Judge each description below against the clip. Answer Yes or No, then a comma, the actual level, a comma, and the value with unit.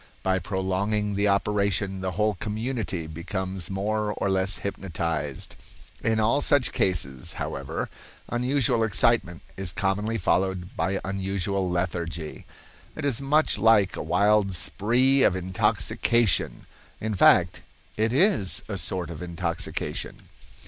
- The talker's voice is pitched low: Yes, low, 100 Hz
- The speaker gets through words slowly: Yes, slow, 120 wpm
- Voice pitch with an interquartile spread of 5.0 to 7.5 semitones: No, average, 3.0 semitones